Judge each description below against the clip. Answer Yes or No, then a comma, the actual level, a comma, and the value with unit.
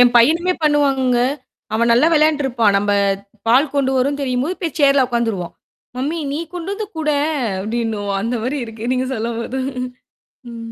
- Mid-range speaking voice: No, very high, 255 Hz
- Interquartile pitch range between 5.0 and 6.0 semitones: No, average, 4.1 semitones